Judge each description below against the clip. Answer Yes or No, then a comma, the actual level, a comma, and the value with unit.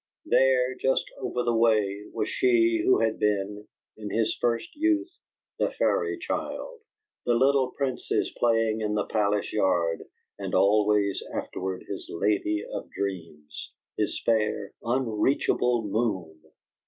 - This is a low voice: Yes, low, 110 Hz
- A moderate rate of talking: No, slow, 130 wpm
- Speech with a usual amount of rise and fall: Yes, average, 3.4 semitones